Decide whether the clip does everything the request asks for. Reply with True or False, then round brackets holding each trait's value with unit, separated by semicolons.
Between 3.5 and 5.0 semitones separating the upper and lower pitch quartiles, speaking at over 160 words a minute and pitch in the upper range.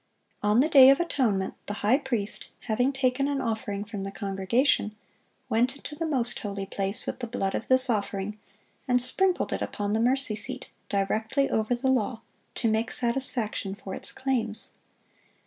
True (4.1 semitones; 170 wpm; 230 Hz)